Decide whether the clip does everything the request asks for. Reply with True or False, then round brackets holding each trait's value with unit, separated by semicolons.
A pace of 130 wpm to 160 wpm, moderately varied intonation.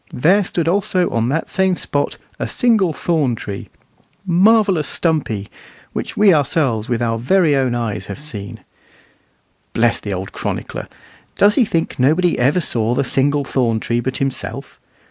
False (155 wpm; 7.1 semitones)